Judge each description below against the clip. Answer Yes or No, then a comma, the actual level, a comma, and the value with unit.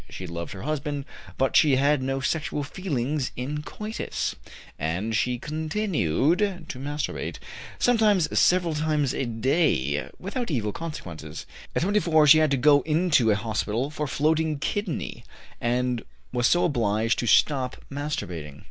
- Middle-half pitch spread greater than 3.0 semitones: Yes, average, 5.0 semitones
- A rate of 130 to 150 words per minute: Yes, average, 140 wpm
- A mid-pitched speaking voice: Yes, medium, 145 Hz